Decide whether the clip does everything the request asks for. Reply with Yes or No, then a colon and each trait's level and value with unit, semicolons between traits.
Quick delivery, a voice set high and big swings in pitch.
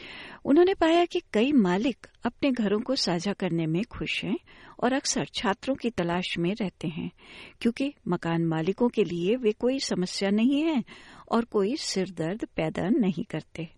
No: average, 160 wpm; high, 215 Hz; wide, 6.6 semitones